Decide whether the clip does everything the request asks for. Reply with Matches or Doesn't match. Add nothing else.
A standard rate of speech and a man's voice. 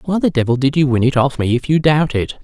Doesn't match